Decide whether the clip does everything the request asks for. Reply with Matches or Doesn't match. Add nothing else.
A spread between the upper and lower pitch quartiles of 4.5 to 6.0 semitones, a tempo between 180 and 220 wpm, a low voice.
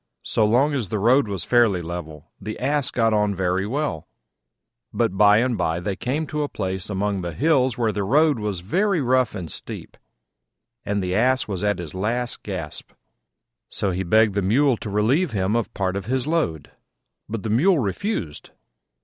Matches